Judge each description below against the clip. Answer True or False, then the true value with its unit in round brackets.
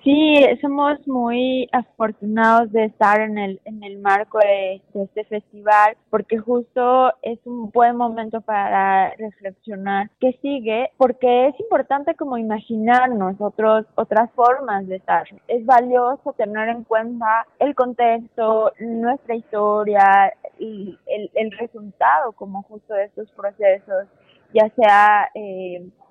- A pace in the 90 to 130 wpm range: True (125 wpm)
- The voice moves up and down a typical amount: True (3.1 semitones)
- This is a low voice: False (225 Hz)